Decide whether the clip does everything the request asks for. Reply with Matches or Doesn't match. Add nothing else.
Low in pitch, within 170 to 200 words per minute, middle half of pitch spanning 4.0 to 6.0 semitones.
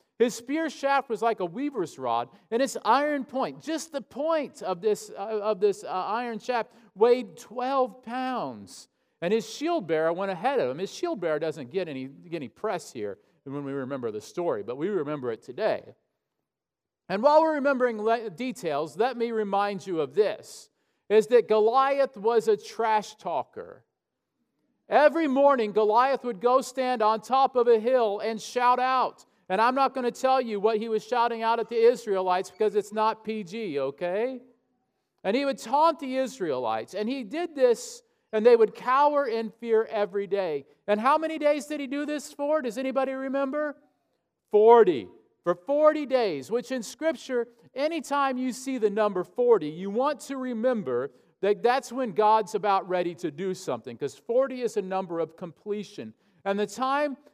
Doesn't match